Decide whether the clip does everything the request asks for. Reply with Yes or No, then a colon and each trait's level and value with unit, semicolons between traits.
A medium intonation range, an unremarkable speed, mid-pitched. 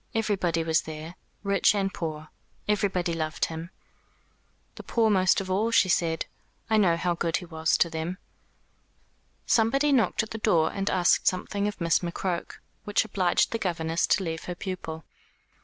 Yes: average, 3.7 semitones; average, 165 wpm; medium, 180 Hz